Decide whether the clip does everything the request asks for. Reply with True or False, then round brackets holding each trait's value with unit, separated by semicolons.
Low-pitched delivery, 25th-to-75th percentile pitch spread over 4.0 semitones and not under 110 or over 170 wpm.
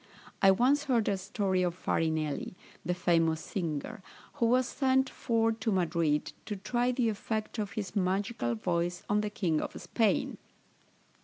False (200 Hz; 4.8 semitones; 155 wpm)